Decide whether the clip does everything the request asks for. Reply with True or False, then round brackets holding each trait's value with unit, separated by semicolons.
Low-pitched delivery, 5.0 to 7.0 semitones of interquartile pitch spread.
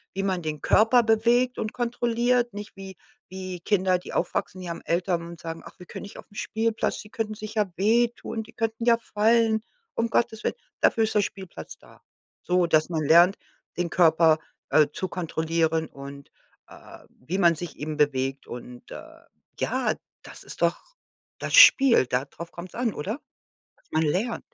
False (190 Hz; 5.3 semitones)